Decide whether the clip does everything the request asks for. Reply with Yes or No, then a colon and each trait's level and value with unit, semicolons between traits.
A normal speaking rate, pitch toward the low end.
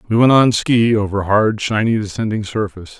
Yes: average, 180 wpm; low, 105 Hz